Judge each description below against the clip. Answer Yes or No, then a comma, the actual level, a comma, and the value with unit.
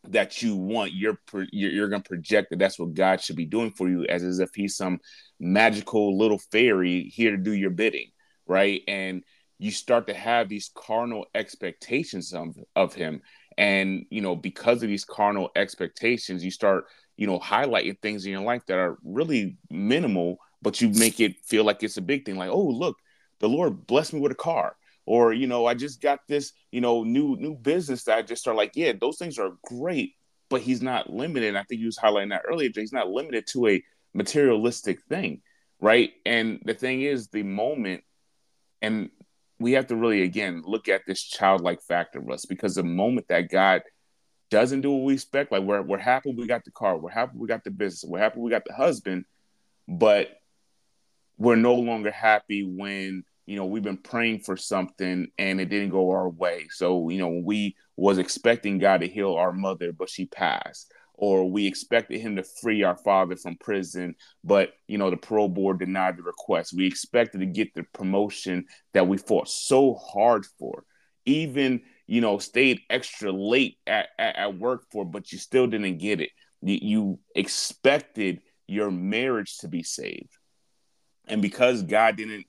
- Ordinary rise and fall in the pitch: Yes, average, 4.0 semitones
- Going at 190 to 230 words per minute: Yes, average, 195 wpm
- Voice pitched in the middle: No, low, 105 Hz